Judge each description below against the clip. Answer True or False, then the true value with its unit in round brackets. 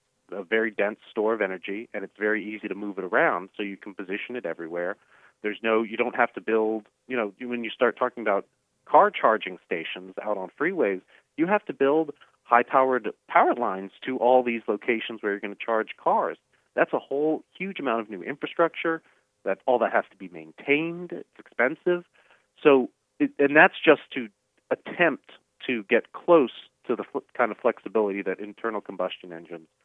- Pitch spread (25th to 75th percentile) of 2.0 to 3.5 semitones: False (5.2 semitones)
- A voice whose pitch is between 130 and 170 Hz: False (115 Hz)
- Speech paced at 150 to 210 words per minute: True (190 wpm)